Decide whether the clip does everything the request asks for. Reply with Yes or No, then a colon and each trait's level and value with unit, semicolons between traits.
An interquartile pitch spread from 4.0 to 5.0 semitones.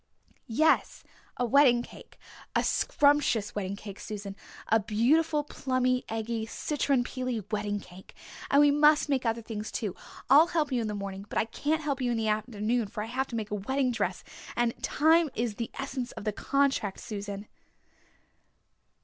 Yes: average, 4.7 semitones